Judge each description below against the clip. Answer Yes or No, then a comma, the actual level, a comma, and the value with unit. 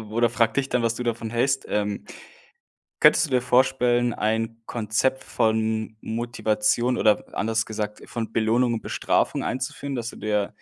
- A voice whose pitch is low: Yes, low, 115 Hz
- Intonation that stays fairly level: Yes, narrow, 2.0 semitones